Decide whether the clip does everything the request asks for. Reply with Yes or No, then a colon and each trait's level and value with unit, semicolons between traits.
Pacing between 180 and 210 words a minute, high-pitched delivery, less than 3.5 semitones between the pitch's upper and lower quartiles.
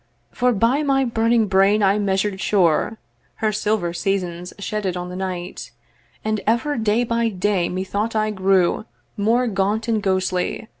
No: average, 150 wpm; high, 205 Hz; average, 3.0 semitones